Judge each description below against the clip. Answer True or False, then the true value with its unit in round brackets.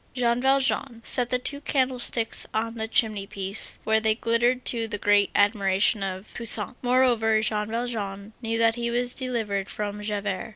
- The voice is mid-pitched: False (225 Hz)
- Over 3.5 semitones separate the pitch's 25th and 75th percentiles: False (2.9 semitones)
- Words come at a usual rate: True (165 wpm)